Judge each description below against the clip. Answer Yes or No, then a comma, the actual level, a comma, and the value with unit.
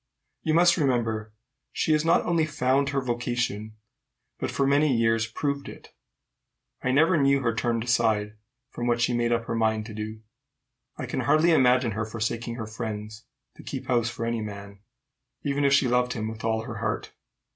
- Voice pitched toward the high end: No, low, 120 Hz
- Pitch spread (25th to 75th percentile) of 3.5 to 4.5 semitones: Yes, average, 3.8 semitones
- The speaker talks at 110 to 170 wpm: No, average, 185 wpm